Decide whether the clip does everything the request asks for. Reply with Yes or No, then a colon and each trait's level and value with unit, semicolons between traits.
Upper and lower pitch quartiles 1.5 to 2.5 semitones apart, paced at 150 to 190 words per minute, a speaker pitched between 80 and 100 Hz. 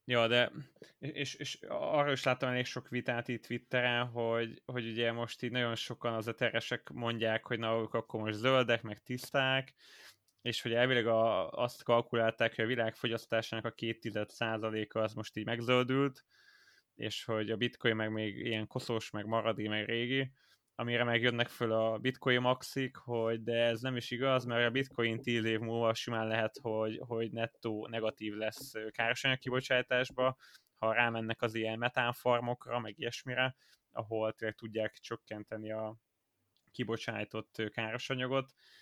No: narrow, 1.9 semitones; fast, 155 wpm; low, 115 Hz